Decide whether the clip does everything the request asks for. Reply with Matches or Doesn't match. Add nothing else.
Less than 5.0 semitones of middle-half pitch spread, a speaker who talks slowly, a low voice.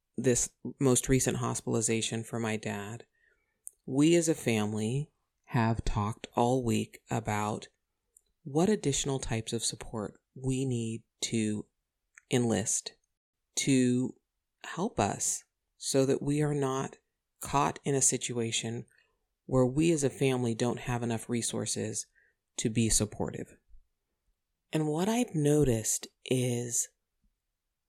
Matches